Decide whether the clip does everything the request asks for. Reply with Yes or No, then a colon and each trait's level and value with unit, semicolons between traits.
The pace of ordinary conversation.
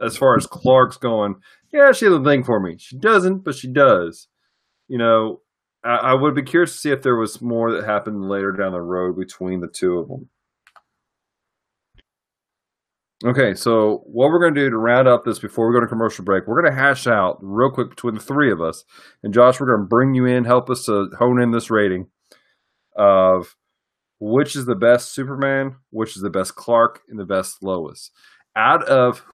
No: fast, 210 wpm